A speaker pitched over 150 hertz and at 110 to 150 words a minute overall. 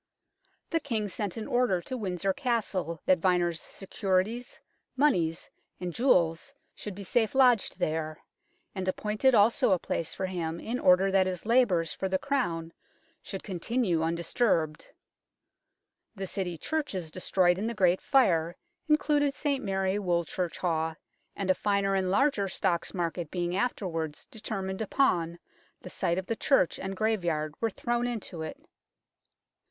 Yes: high, 190 Hz; average, 145 wpm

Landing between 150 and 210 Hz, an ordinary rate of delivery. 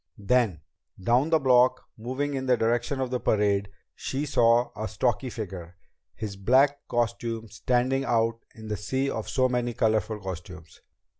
No: low, 120 Hz; average, 155 wpm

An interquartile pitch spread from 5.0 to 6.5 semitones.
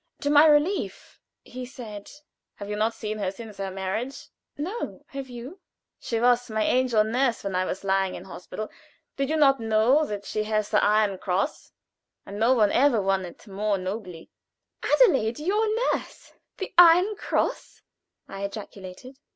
Yes: average, 5.3 semitones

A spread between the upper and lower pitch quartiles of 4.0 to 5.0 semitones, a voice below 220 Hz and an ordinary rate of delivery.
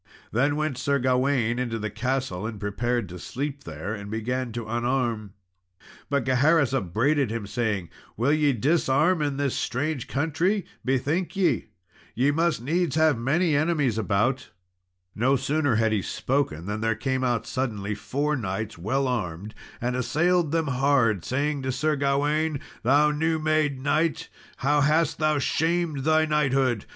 Yes: average, 4.6 semitones; low, 135 Hz; average, 155 wpm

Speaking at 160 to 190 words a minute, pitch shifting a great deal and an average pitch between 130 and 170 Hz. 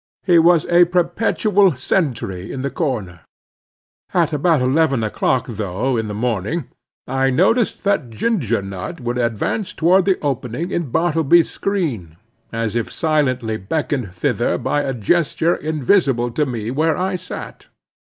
No: average, 140 wpm; wide, 6.8 semitones; low, 135 Hz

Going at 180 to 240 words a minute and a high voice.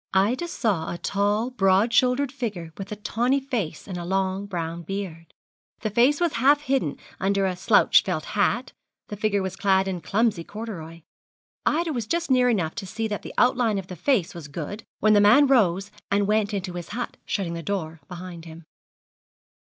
Yes: average, 190 wpm; high, 200 Hz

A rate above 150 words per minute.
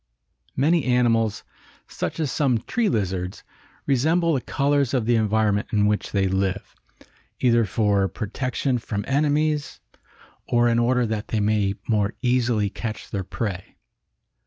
No: slow, 135 wpm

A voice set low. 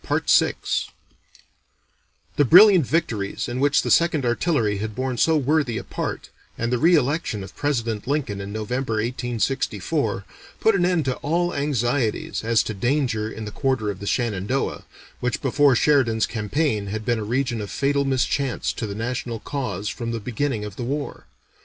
Yes: low, 125 Hz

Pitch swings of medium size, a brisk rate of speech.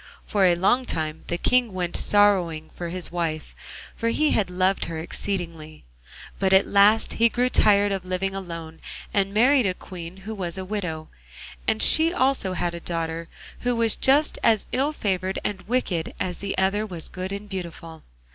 No: average, 3.6 semitones; average, 180 wpm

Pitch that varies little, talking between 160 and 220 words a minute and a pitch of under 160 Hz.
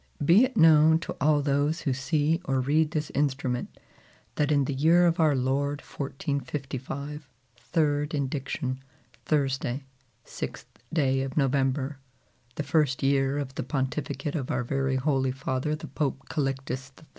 No: narrow, 2.1 semitones; average, 145 wpm; medium, 140 Hz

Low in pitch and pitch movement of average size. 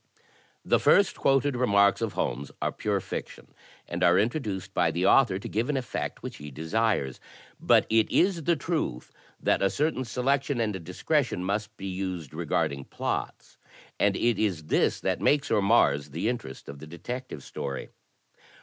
No: low, 105 Hz; wide, 6.9 semitones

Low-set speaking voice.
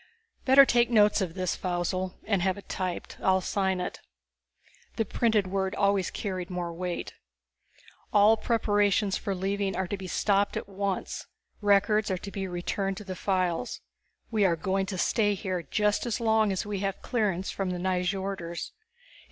No: high, 195 Hz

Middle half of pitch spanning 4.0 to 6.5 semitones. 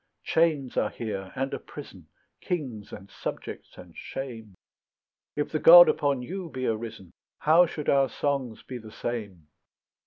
Yes: average, 5.2 semitones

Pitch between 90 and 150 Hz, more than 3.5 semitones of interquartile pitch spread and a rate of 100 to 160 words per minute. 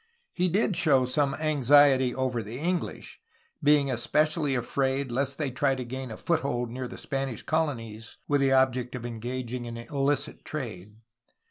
No: low, 135 Hz; average, 3.0 semitones; average, 155 wpm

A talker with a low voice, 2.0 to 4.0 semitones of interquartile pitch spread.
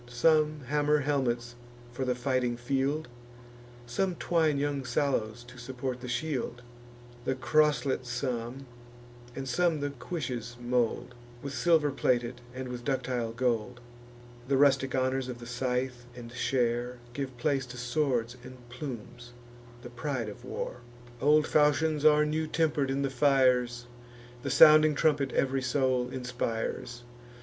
Yes: low, 130 Hz; average, 2.8 semitones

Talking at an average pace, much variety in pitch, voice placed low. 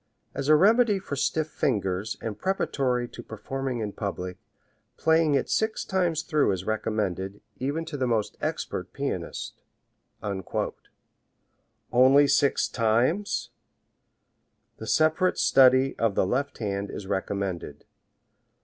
No: slow, 120 wpm; wide, 7.0 semitones; low, 130 Hz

